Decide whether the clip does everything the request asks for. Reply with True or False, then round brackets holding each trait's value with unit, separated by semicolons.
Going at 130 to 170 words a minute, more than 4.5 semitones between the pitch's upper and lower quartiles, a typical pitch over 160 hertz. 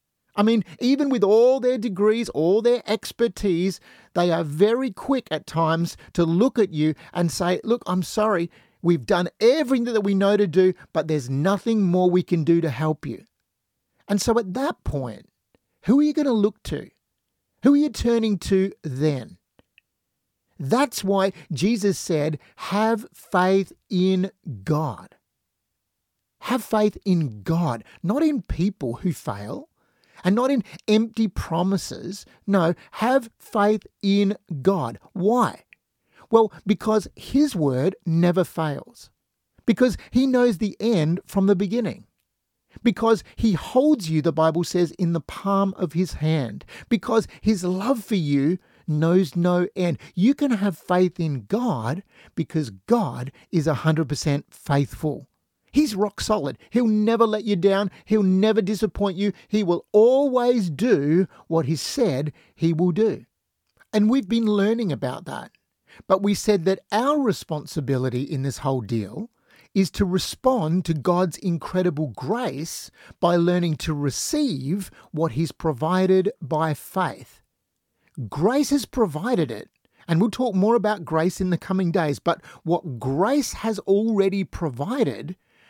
True (145 wpm; 5.0 semitones; 190 Hz)